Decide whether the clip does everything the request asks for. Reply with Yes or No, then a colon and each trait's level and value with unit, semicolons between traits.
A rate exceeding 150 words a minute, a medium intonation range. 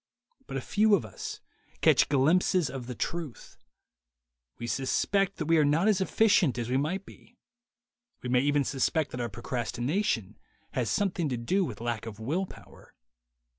No: average, 170 wpm; wide, 7.3 semitones